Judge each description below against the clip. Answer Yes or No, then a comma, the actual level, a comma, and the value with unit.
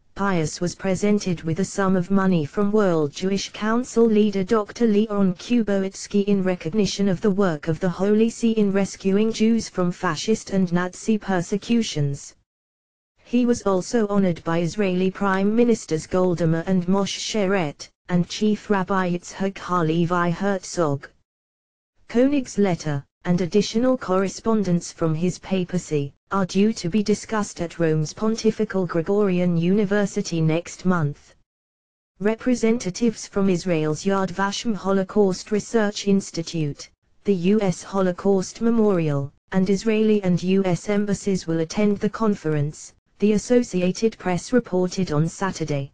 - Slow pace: Yes, slow, 130 wpm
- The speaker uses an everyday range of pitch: Yes, average, 3.3 semitones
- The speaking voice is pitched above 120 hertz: Yes, high, 190 Hz